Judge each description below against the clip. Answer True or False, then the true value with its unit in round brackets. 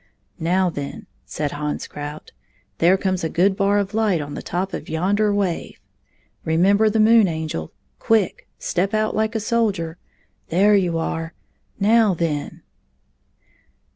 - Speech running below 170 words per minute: True (155 wpm)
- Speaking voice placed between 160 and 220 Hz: True (190 Hz)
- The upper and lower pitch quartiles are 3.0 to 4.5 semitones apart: True (4.2 semitones)